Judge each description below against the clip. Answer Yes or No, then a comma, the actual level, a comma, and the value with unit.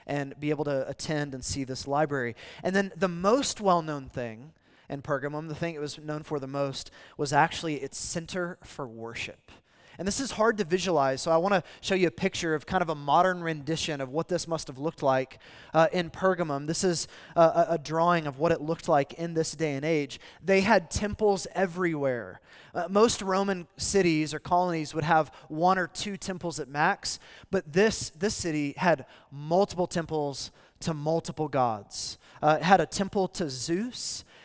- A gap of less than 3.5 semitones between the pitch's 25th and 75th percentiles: No, average, 3.9 semitones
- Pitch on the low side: No, medium, 160 Hz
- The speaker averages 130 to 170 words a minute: No, average, 195 wpm